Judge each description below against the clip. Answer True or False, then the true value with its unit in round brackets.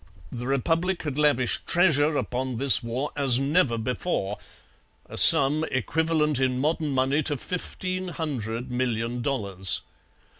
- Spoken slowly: True (125 wpm)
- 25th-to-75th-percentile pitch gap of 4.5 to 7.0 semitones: False (4.1 semitones)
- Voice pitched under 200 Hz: True (135 Hz)